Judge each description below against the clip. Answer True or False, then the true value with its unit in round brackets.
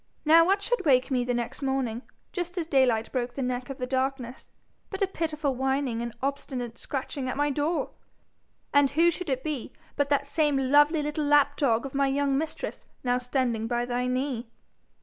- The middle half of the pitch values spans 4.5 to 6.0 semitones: False (2.8 semitones)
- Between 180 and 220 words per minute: True (190 wpm)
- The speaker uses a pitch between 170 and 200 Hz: False (270 Hz)